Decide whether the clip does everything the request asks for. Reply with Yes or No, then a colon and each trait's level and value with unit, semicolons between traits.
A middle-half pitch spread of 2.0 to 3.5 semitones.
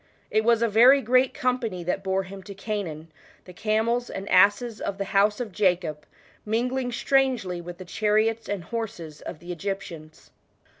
No: average, 4.2 semitones